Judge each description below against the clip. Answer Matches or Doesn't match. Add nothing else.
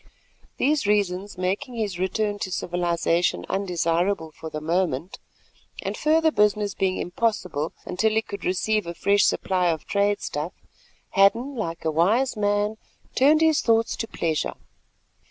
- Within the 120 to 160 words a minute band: Matches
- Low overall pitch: Doesn't match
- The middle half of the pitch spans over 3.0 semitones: Matches